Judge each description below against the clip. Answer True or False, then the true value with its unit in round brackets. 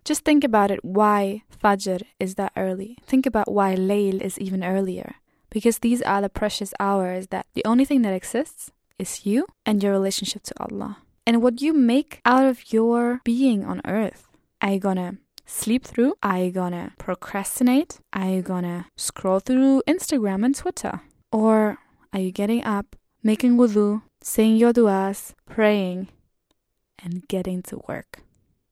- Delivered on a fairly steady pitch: False (4.0 semitones)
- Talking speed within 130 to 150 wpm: False (160 wpm)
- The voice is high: True (210 Hz)